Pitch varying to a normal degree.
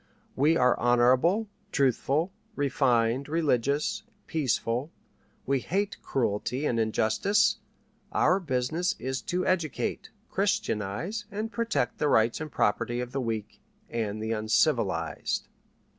No: wide, 6.0 semitones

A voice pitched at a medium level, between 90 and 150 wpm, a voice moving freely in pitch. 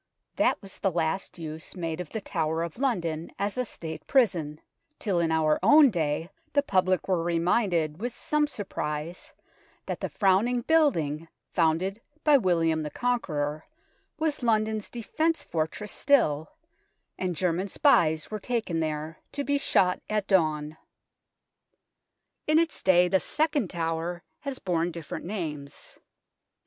Yes: medium, 180 Hz; average, 140 wpm; wide, 5.8 semitones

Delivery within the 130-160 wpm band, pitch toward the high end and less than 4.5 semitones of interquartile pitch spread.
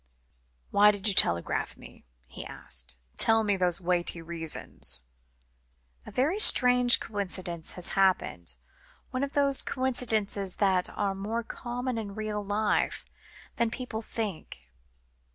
No: slow, 135 wpm; high, 200 Hz; average, 5.2 semitones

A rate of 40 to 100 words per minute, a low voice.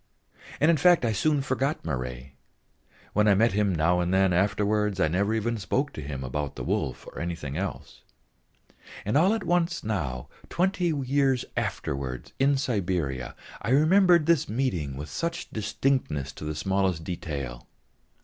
No: average, 160 wpm; low, 100 Hz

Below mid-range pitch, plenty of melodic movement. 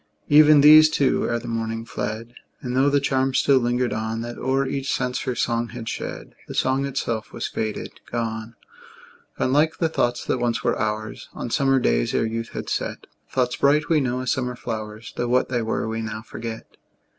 No: low, 120 Hz; average, 3.0 semitones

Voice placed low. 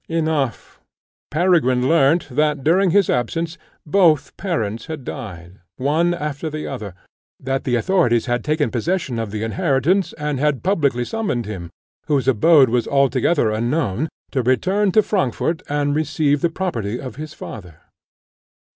No: medium, 145 Hz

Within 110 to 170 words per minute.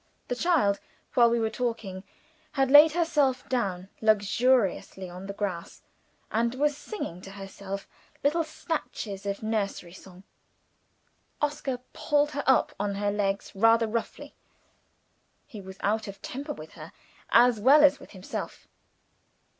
Yes: average, 140 wpm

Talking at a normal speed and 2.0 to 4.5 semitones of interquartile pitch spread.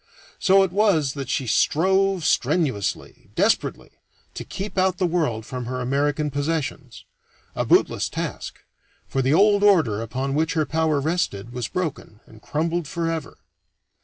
No: average, 145 wpm; wide, 5.4 semitones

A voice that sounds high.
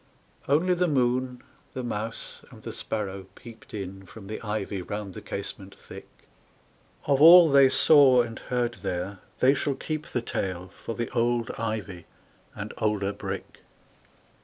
No: low, 115 Hz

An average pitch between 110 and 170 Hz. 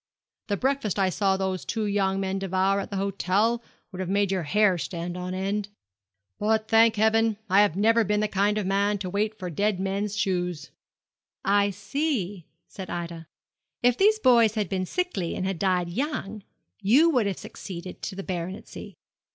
No: high, 200 Hz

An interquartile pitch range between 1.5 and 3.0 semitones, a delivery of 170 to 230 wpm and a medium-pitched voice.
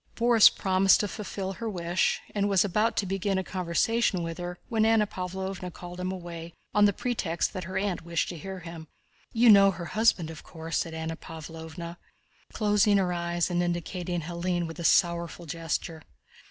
Yes: average, 2.7 semitones; average, 180 wpm; medium, 180 Hz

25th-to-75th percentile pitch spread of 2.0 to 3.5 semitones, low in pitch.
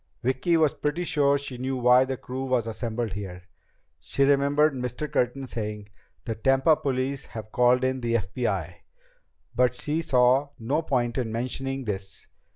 Yes: average, 2.9 semitones; low, 125 Hz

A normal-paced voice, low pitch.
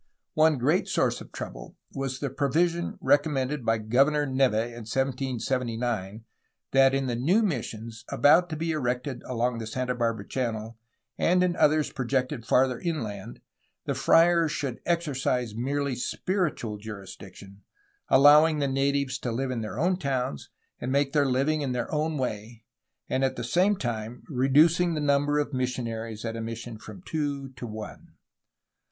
Yes: average, 160 wpm; low, 130 Hz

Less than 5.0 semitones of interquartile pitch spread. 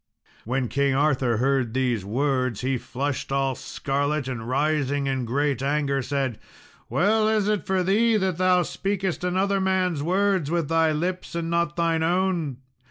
No: wide, 5.4 semitones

